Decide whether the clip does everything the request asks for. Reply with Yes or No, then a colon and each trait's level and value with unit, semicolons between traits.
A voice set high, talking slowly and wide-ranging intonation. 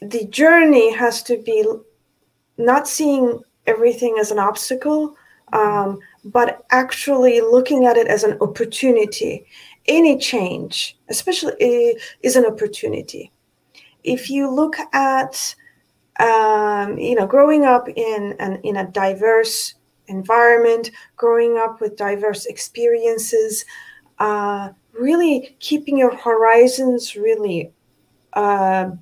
Yes: high, 240 Hz; slow, 110 wpm; wide, 5.7 semitones